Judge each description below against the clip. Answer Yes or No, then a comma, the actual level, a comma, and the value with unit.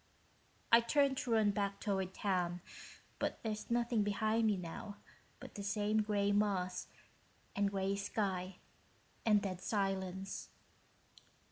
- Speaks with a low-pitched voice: No, high, 200 Hz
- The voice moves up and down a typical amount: No, narrow, 2.1 semitones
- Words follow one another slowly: Yes, slow, 125 wpm